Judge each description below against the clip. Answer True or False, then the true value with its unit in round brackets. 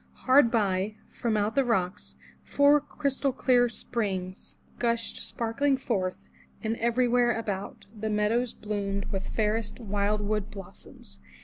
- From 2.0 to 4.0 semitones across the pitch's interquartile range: True (3.2 semitones)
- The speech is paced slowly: True (130 wpm)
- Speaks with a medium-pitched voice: False (220 Hz)